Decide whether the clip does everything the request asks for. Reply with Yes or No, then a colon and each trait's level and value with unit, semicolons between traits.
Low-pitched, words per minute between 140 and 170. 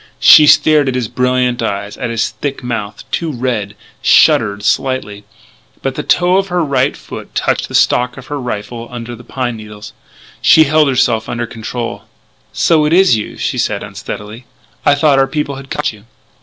No: low, 125 Hz; average, 180 wpm